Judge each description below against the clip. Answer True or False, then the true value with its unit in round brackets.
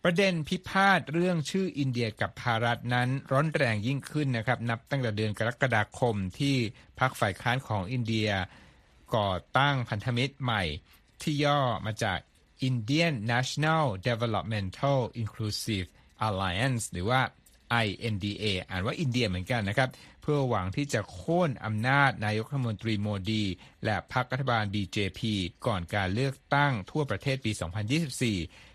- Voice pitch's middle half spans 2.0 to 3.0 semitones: False (4.5 semitones)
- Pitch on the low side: True (120 Hz)